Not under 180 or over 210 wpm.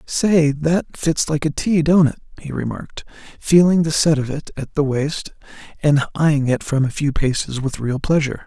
Yes: average, 200 wpm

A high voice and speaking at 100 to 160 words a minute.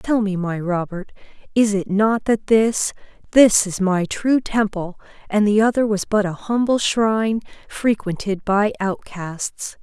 Yes: high, 205 Hz; average, 155 wpm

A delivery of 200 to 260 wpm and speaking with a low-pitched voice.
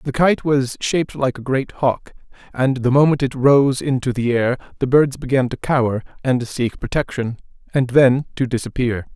No: average, 175 wpm; low, 130 Hz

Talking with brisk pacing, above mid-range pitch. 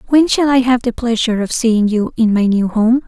Yes: fast, 255 wpm; high, 235 Hz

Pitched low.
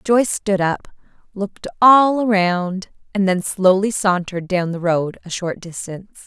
No: high, 190 Hz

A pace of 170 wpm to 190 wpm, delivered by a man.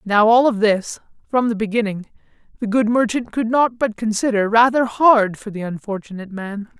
Yes: average, 175 wpm; male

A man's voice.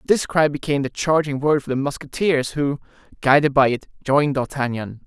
Yes: male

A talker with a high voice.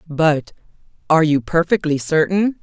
No: medium, 165 Hz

